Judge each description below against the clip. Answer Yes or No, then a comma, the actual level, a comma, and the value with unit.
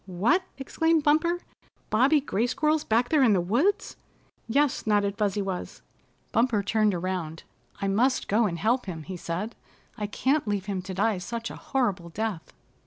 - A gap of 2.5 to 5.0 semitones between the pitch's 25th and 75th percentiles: No, wide, 5.5 semitones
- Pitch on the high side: Yes, high, 215 Hz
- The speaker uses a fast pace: No, average, 170 wpm